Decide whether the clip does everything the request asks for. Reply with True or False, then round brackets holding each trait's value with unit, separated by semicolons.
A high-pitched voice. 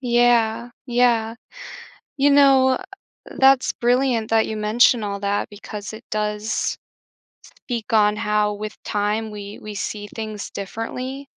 True (220 Hz)